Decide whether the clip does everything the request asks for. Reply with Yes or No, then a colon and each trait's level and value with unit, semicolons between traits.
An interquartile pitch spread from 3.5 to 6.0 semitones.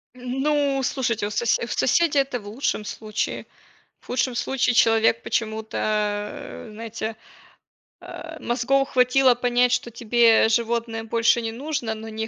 No: narrow, 2.5 semitones